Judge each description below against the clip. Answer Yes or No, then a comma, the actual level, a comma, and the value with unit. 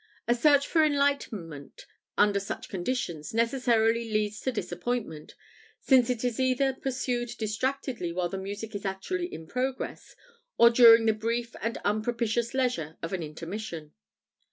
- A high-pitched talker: Yes, high, 230 Hz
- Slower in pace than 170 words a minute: Yes, average, 140 wpm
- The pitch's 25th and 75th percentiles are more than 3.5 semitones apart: Yes, average, 4.1 semitones